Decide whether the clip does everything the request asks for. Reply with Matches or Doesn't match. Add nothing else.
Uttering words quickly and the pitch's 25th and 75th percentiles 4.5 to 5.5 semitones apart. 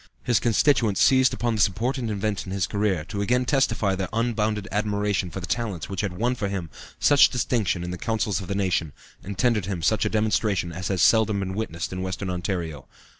Doesn't match